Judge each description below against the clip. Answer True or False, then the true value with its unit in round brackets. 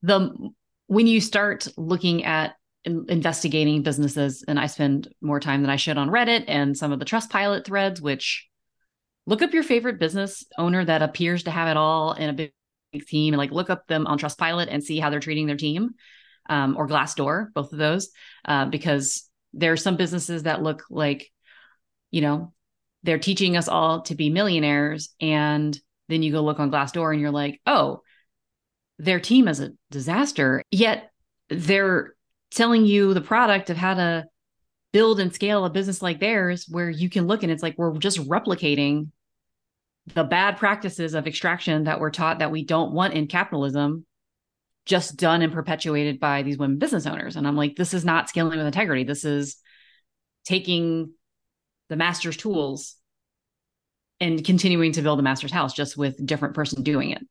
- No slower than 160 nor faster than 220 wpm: True (185 wpm)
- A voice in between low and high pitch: True (160 Hz)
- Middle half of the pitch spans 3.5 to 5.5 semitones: True (3.8 semitones)